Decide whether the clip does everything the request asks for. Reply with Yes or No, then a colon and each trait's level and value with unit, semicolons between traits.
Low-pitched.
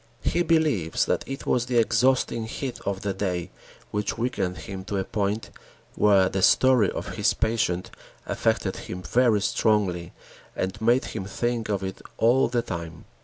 Yes: low, 105 Hz